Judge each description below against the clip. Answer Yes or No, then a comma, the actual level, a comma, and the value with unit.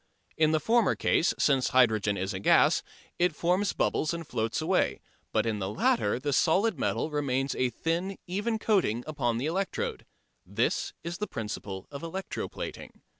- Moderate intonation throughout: No, wide, 7.4 semitones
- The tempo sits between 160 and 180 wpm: Yes, average, 170 wpm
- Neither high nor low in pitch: Yes, medium, 150 Hz